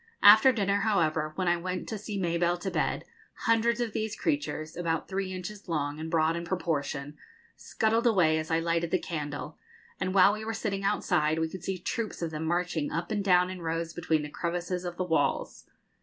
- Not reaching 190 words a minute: No, average, 200 wpm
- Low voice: No, medium, 175 Hz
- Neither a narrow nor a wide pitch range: Yes, average, 3.5 semitones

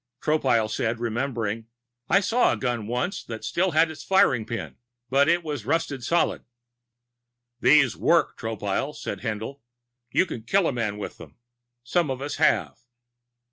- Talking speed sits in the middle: Yes, average, 155 wpm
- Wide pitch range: Yes, wide, 5.9 semitones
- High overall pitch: No, low, 130 Hz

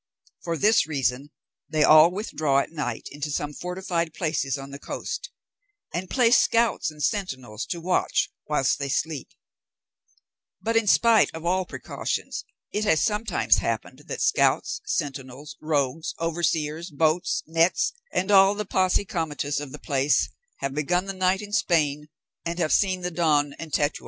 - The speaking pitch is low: No, medium, 165 Hz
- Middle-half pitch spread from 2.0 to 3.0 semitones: No, average, 4.3 semitones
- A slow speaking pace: No, average, 155 wpm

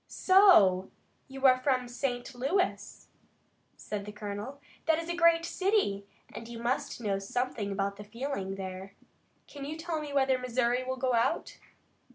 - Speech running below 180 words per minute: Yes, average, 160 wpm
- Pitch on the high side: Yes, very high, 250 Hz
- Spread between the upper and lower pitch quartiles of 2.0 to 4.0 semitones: No, wide, 5.5 semitones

